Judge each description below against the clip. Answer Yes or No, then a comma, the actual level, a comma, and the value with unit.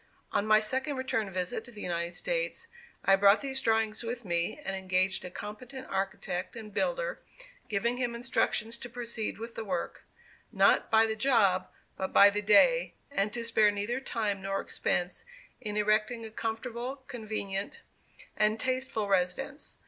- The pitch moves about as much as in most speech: Yes, average, 3.7 semitones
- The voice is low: No, high, 220 Hz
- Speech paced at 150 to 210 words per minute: Yes, average, 160 wpm